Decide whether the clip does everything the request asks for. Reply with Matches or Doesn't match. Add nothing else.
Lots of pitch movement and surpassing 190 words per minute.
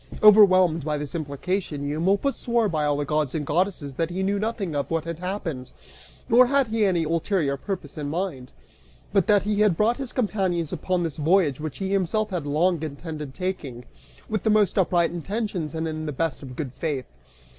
Doesn't match